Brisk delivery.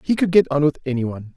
Yes: fast, 265 wpm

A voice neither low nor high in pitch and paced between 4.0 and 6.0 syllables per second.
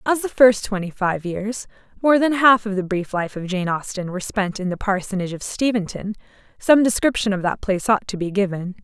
No: high, 205 Hz; 5.6 syllables/s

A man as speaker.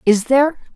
No: female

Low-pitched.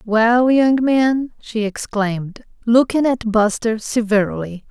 No: high, 230 Hz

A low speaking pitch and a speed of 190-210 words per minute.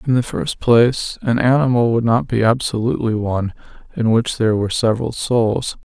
No: low, 115 Hz; average, 170 wpm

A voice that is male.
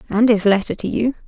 No: female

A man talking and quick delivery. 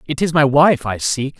Yes: male; fast, 255 wpm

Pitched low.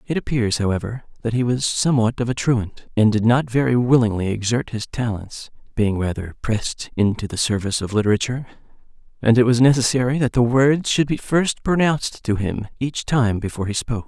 Yes: low, 120 Hz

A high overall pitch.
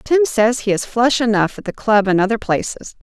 Yes: high, 225 Hz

